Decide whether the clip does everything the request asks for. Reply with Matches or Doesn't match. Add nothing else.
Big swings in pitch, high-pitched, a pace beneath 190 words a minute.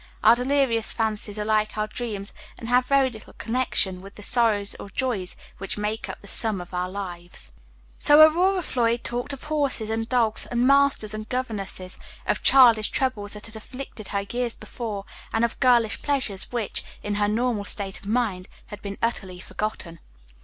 Doesn't match